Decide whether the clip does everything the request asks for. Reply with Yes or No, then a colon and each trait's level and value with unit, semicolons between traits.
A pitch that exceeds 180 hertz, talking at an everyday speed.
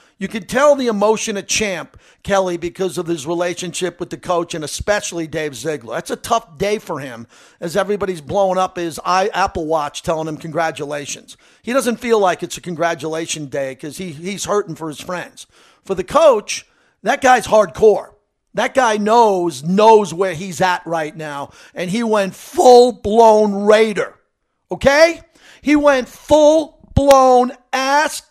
Yes: high, 190 Hz; average, 160 wpm